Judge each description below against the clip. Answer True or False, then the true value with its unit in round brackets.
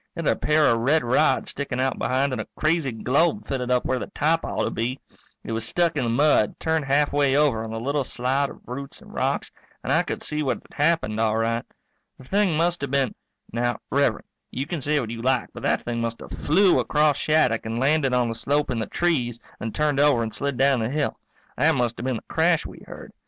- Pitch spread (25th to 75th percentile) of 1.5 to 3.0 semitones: False (4.3 semitones)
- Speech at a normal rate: False (240 wpm)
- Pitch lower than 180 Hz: True (135 Hz)